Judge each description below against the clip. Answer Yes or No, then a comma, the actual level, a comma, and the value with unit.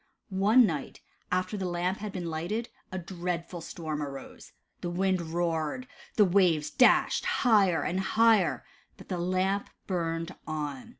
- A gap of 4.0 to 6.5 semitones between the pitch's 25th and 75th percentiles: No, average, 2.8 semitones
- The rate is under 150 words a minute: Yes, average, 140 wpm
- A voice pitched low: No, medium, 180 Hz